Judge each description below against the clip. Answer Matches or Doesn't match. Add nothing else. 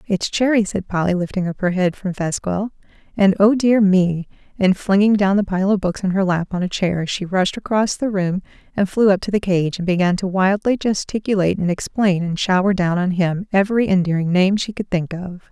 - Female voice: Matches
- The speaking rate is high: Matches